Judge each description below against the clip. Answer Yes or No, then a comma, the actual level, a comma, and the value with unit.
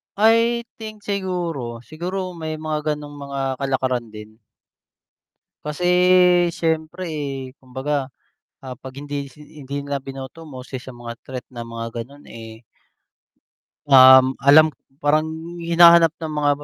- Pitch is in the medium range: Yes, medium, 145 Hz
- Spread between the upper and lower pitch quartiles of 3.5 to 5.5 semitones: Yes, average, 3.8 semitones